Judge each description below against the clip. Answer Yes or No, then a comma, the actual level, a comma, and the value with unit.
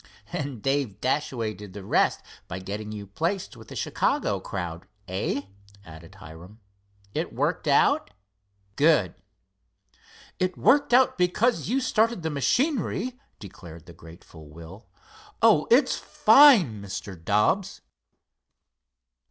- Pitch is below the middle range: Yes, low, 110 Hz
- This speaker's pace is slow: Yes, slow, 120 wpm